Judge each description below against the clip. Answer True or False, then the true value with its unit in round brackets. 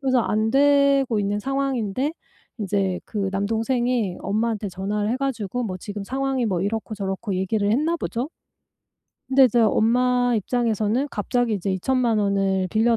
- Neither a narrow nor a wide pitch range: True (3.9 semitones)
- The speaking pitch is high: True (225 Hz)